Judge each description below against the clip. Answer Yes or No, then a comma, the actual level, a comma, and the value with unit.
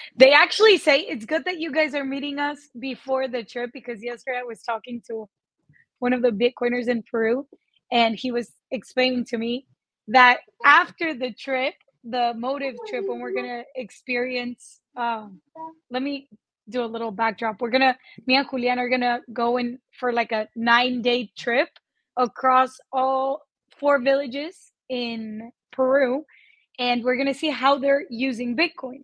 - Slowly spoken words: No, average, 170 wpm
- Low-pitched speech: No, very high, 250 Hz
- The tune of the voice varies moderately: No, narrow, 2.3 semitones